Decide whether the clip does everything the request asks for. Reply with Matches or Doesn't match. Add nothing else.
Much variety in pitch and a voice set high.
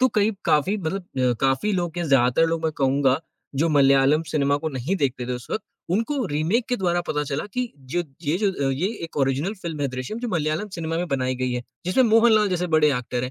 Doesn't match